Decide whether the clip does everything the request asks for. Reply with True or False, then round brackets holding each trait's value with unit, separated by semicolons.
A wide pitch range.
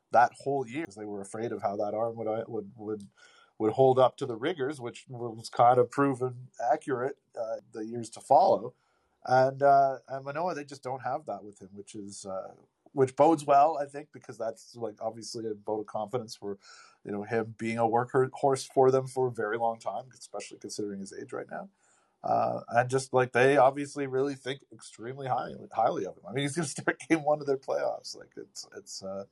False (3.8 semitones)